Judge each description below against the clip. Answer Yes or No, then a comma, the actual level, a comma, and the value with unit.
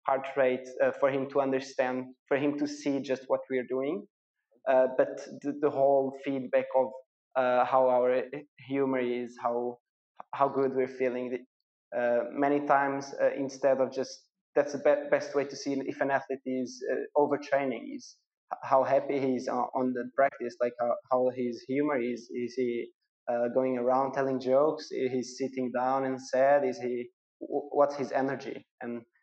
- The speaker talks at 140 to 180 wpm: Yes, average, 175 wpm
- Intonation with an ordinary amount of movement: No, narrow, 1.6 semitones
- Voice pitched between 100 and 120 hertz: No, low, 130 Hz